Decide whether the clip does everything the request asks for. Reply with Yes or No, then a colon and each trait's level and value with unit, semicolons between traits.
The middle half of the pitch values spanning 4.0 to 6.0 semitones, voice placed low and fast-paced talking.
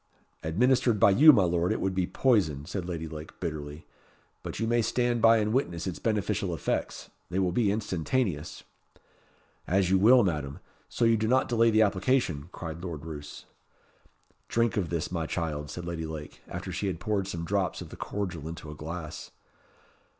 No: average, 5.0 semitones; very low, 90 Hz; average, 180 wpm